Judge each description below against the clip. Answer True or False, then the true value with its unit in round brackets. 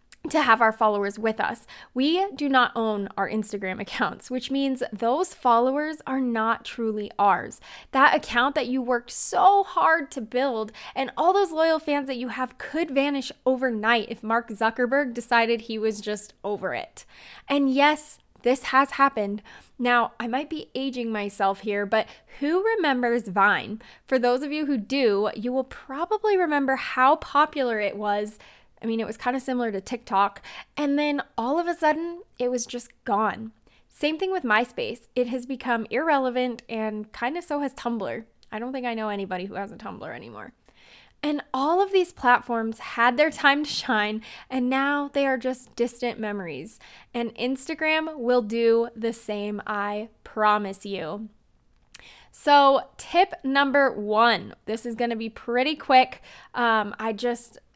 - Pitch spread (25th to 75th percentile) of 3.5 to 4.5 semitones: True (4.2 semitones)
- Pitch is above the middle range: True (245 Hz)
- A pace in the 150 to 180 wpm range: True (170 wpm)